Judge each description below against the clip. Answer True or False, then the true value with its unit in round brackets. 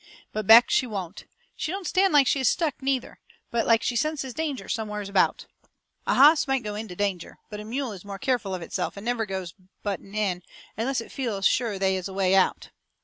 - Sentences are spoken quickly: True (220 wpm)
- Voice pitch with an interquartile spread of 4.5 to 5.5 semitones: True (5.2 semitones)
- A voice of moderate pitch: False (220 Hz)